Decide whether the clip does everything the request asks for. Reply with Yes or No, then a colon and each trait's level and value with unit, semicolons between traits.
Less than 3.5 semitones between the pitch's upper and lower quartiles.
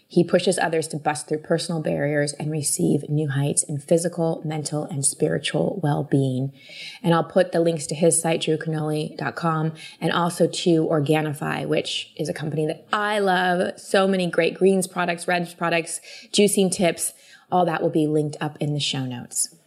Yes: narrow, 2.5 semitones